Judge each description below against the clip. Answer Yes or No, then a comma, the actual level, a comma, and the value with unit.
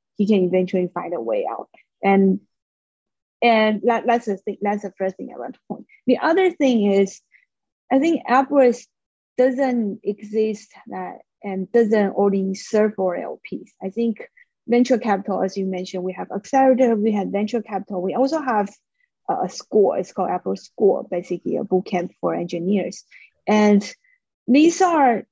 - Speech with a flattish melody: No, average, 4.9 semitones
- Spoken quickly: No, average, 165 wpm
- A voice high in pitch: Yes, high, 215 Hz